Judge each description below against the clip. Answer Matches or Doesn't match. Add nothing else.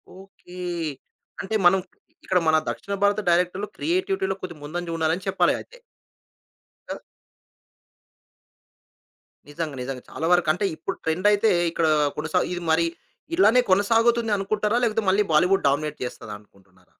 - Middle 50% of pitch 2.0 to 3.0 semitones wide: Doesn't match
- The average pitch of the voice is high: Doesn't match